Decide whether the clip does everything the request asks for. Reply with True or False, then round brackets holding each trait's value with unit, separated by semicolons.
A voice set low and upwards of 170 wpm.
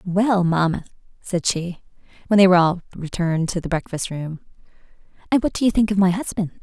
False (185 Hz; 190 wpm)